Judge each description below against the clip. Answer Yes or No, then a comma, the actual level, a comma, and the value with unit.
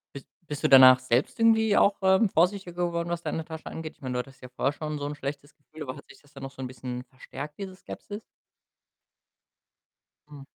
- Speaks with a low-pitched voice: No, medium, 150 Hz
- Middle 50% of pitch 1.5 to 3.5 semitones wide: No, average, 4.7 semitones